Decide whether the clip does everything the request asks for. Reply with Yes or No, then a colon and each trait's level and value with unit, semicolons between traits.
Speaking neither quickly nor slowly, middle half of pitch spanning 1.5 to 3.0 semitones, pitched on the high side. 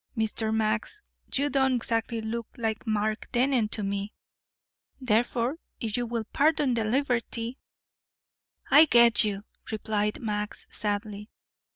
No: slow, 130 wpm; narrow, 2.5 semitones; high, 225 Hz